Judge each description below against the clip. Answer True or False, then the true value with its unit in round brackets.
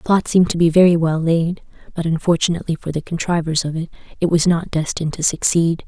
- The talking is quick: True (215 wpm)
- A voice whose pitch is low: False (165 Hz)